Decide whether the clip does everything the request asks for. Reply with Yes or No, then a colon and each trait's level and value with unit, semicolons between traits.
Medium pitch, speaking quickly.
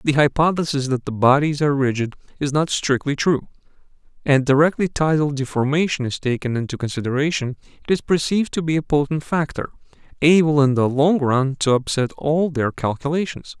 No: medium, 145 Hz; average, 165 wpm